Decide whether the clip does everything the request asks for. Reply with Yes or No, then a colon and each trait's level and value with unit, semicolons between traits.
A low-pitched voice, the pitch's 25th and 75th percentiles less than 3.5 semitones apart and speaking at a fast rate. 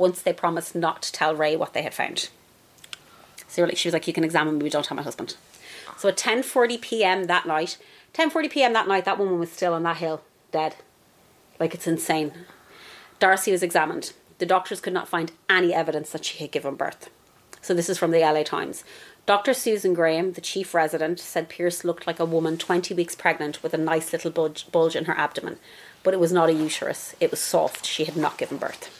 No: medium, 170 Hz; narrow, 2.5 semitones; fast, 215 wpm